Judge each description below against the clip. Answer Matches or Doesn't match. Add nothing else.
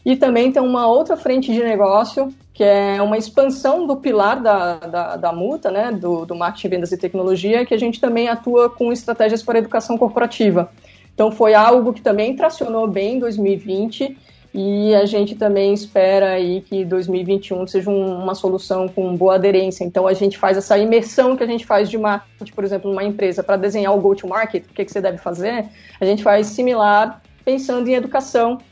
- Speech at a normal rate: Doesn't match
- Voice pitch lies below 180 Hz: Doesn't match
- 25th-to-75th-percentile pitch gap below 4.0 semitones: Matches